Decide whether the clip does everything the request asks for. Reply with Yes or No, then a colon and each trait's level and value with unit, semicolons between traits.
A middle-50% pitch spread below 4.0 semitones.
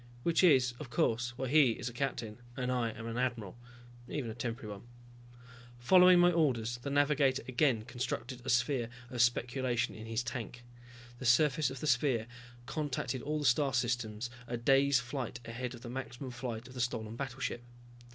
Yes: narrow, 2.4 semitones